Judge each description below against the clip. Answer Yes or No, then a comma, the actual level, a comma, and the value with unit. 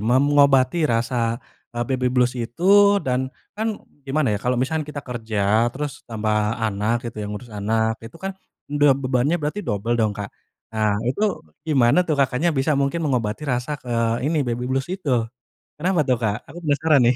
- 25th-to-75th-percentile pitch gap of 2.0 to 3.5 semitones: No, average, 4.1 semitones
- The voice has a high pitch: No, low, 130 Hz